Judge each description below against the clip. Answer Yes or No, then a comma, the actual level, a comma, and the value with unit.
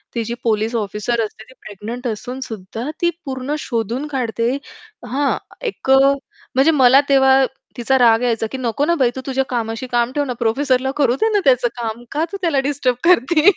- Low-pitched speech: No, very high, 255 Hz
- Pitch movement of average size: Yes, average, 3.2 semitones